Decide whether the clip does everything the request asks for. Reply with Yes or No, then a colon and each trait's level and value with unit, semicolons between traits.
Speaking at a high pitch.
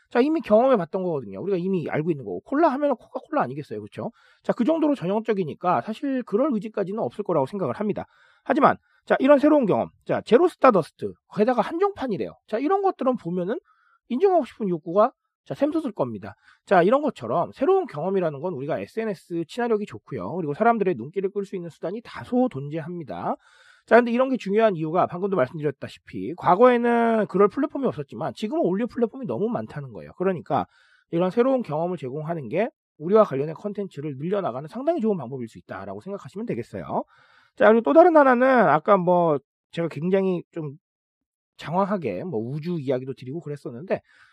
Yes: high, 205 Hz